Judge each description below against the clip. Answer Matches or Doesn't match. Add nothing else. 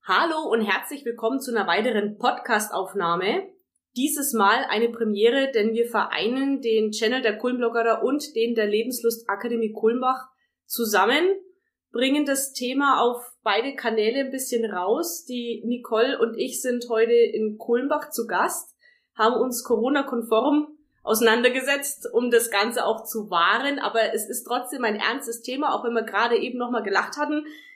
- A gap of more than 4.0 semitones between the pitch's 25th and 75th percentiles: Doesn't match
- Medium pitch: Doesn't match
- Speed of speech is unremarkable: Matches